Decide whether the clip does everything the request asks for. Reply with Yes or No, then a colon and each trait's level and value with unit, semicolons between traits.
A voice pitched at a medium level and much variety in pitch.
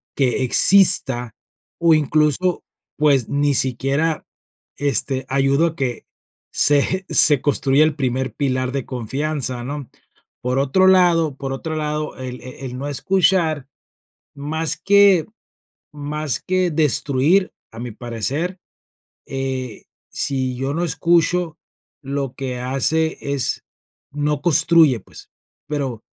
No: medium, 145 Hz; average, 3.4 semitones